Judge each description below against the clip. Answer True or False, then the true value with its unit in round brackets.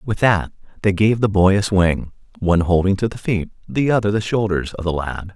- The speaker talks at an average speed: False (225 wpm)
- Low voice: True (100 Hz)